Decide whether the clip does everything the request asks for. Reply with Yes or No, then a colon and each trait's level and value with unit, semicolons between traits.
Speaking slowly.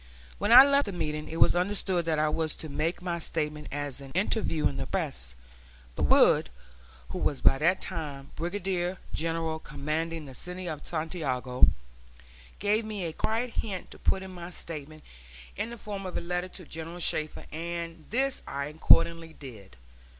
No: average, 170 wpm